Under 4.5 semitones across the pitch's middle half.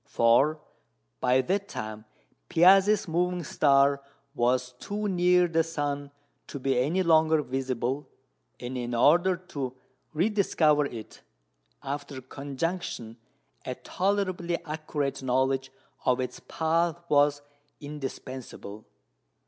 No: average, 4.8 semitones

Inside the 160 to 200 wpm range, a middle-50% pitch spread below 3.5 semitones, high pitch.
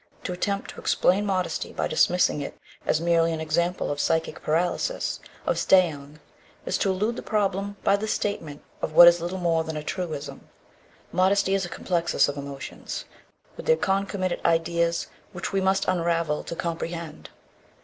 No: average, 165 wpm; average, 2.9 semitones; medium, 175 Hz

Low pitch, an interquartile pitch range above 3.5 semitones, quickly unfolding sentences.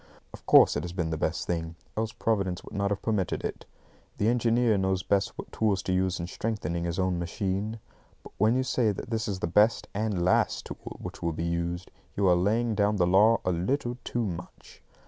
Yes: very low, 95 Hz; average, 4.0 semitones; fast, 215 wpm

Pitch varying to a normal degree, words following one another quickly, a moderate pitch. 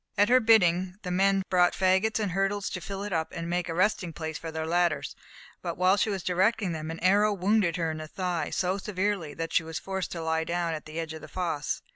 Yes: average, 3.1 semitones; fast, 245 wpm; medium, 180 Hz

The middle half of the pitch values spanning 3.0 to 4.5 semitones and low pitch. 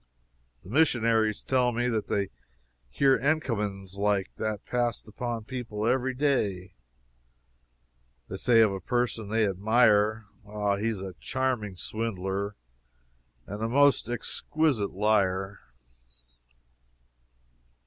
Yes: average, 3.4 semitones; low, 110 Hz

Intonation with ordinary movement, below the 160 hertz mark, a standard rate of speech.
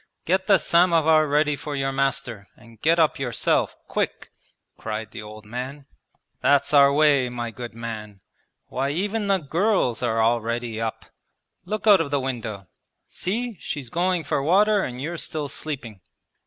No: wide, 6.0 semitones; medium, 140 Hz; average, 155 wpm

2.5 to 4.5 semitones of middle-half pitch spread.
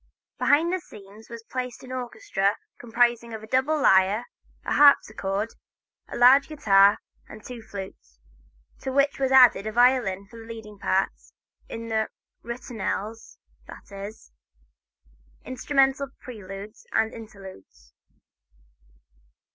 Yes: average, 4.2 semitones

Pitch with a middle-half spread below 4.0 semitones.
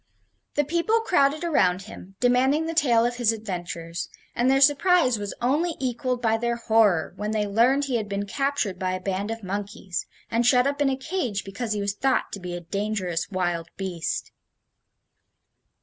No: wide, 5.5 semitones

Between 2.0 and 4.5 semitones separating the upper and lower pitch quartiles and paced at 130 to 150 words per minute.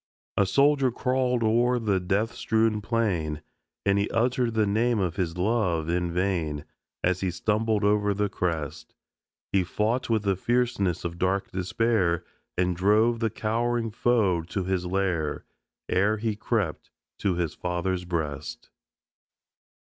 Yes: average, 4.2 semitones; average, 140 wpm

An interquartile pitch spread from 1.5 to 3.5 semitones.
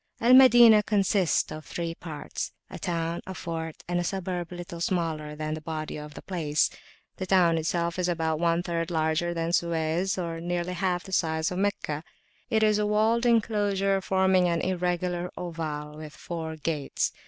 Yes: average, 2.8 semitones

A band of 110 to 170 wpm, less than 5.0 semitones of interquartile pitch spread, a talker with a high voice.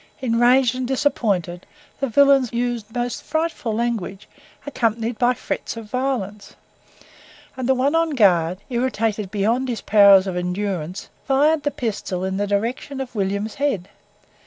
Yes: average, 140 wpm; average, 4.5 semitones; high, 230 Hz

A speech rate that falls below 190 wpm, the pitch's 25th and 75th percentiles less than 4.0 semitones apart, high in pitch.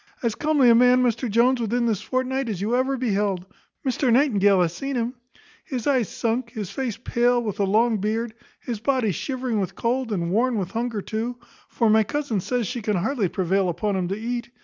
No: fast, 205 wpm; average, 3.4 semitones; high, 230 Hz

